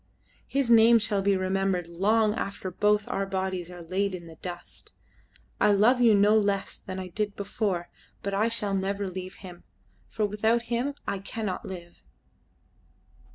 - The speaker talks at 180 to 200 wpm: No, average, 160 wpm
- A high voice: Yes, high, 200 Hz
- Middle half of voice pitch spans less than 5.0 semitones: Yes, narrow, 2.4 semitones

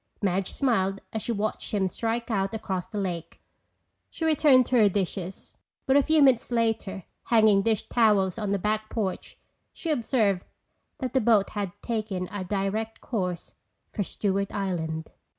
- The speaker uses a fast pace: No, average, 160 wpm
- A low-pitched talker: No, high, 210 Hz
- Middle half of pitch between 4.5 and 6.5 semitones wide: No, average, 3.2 semitones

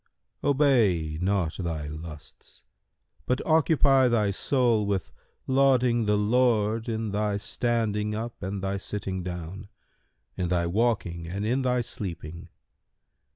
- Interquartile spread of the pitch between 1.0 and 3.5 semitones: No, average, 4.8 semitones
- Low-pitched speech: Yes, low, 105 Hz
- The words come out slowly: Yes, slow, 120 wpm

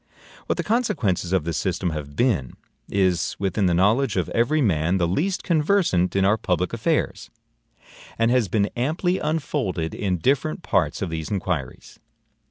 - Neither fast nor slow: Yes, average, 160 wpm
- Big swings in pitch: Yes, wide, 7.7 semitones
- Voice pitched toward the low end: Yes, low, 100 Hz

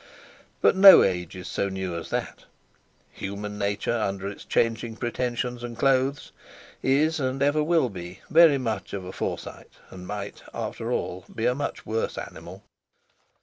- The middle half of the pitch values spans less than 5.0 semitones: No, wide, 5.4 semitones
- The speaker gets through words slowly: No, average, 155 wpm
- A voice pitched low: Yes, low, 115 Hz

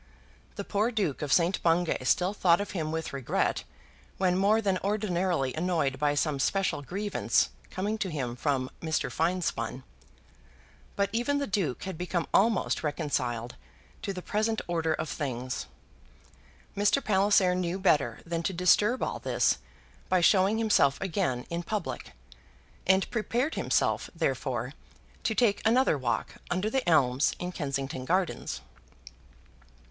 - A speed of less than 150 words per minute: Yes, average, 140 wpm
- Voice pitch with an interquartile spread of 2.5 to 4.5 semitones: No, wide, 5.5 semitones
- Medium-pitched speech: Yes, medium, 180 Hz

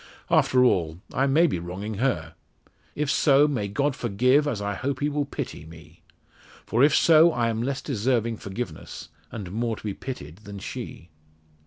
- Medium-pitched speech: No, low, 115 Hz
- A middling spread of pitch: No, wide, 5.8 semitones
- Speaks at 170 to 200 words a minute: Yes, average, 175 wpm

